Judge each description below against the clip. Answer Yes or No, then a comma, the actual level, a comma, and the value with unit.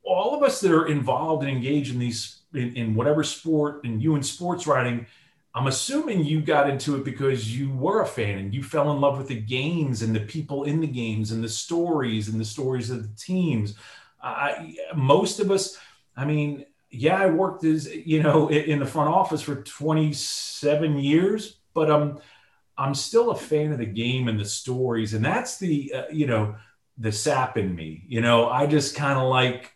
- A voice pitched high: No, medium, 140 Hz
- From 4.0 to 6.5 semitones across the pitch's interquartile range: Yes, average, 4.4 semitones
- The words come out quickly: Yes, fast, 210 wpm